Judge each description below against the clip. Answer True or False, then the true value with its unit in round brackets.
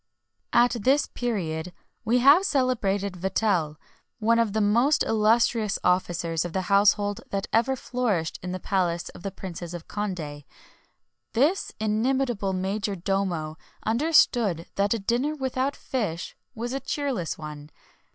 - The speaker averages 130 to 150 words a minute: True (140 wpm)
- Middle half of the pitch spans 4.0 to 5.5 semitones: True (5.1 semitones)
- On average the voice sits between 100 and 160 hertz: False (205 Hz)